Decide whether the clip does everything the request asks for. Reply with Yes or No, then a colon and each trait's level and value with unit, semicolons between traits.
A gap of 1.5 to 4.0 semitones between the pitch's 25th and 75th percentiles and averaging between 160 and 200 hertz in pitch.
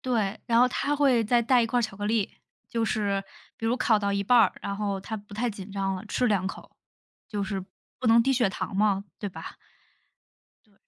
No: average, 2.9 semitones; high, 215 Hz